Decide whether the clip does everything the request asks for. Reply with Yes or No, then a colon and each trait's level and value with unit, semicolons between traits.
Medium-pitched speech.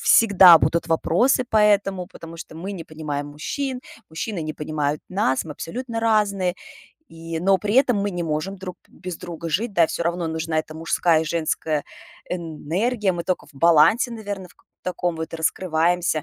Yes: medium, 170 Hz